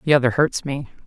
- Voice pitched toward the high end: No, medium, 140 Hz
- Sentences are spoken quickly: Yes, fast, 225 wpm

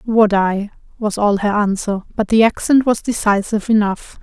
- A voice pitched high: Yes, high, 210 Hz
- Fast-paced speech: No, average, 170 wpm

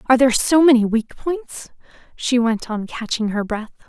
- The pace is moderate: Yes, average, 185 wpm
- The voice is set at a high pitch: Yes, high, 245 Hz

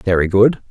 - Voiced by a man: Yes, male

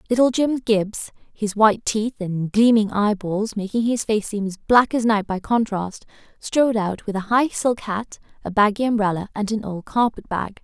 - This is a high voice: Yes, high, 215 Hz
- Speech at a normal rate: Yes, average, 190 wpm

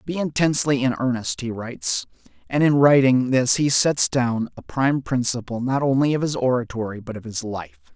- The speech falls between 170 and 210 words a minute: Yes, average, 190 wpm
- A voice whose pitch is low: Yes, low, 130 Hz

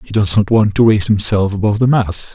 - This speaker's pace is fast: Yes, fast, 255 wpm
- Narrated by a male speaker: Yes, male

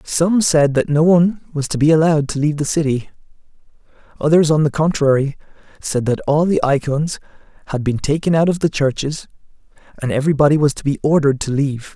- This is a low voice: No, medium, 150 Hz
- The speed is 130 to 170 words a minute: No, average, 185 wpm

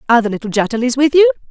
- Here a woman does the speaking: Yes, female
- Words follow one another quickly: Yes, fast, 240 wpm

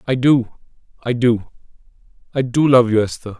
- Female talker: No, male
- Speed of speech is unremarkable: Yes, average, 160 wpm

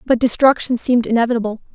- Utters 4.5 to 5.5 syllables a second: No, 7.2 syllables/s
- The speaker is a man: No, female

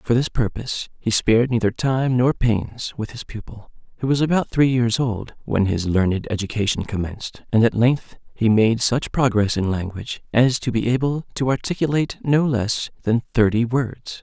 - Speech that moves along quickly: No, average, 180 wpm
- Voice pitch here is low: Yes, low, 120 Hz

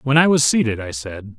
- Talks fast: Yes, fast, 260 wpm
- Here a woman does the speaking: No, male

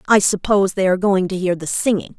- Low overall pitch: No, high, 190 Hz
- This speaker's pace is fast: Yes, fast, 245 wpm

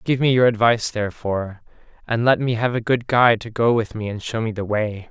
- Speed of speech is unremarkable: No, fast, 245 wpm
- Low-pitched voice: Yes, low, 115 Hz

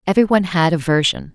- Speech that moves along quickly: No, average, 180 wpm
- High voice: No, medium, 175 Hz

